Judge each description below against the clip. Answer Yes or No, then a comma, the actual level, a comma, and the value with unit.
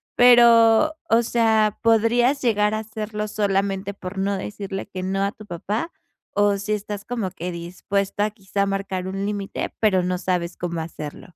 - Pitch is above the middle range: Yes, high, 205 Hz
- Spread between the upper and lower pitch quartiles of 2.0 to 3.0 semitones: Yes, narrow, 2.5 semitones